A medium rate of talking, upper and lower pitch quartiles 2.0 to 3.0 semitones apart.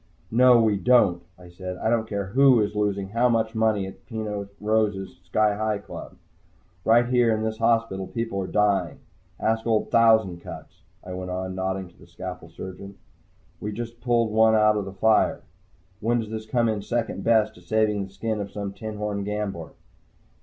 Yes: average, 185 wpm; narrow, 2.6 semitones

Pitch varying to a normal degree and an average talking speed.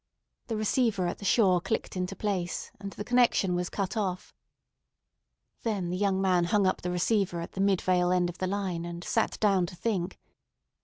No: narrow, 2.3 semitones; average, 190 wpm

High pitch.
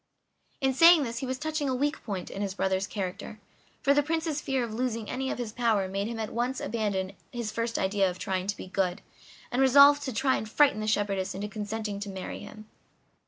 Yes: high, 225 Hz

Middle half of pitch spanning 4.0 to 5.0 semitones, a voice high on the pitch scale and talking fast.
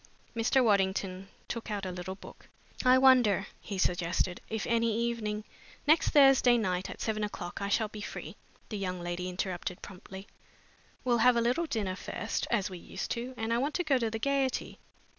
No: average, 4.3 semitones; high, 215 Hz; average, 190 wpm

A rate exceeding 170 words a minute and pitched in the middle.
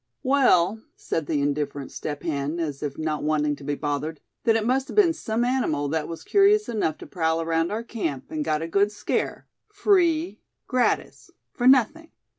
Yes: average, 185 wpm; medium, 170 Hz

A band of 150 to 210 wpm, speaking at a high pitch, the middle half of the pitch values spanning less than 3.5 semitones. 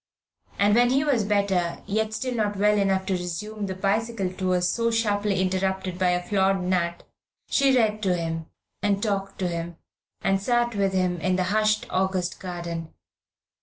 Yes: average, 170 wpm; high, 195 Hz; average, 2.7 semitones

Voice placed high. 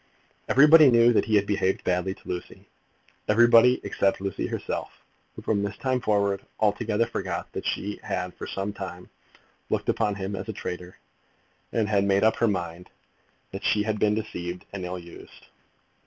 No: low, 100 Hz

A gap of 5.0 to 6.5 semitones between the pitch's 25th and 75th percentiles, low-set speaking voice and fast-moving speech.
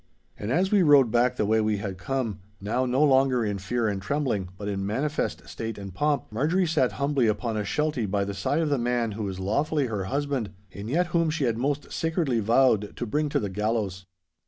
Yes: wide, 5.6 semitones; low, 120 Hz; fast, 210 wpm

